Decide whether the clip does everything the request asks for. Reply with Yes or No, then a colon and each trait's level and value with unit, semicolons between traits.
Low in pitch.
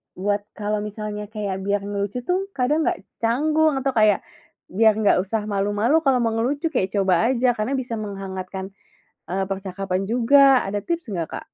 No: high, 210 Hz